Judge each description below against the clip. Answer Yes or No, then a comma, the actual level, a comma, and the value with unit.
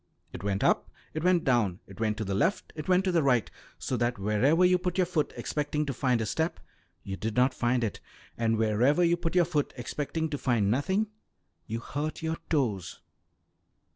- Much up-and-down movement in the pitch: Yes, wide, 6.6 semitones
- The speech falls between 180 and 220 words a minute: Yes, average, 200 wpm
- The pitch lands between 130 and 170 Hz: Yes, low, 135 Hz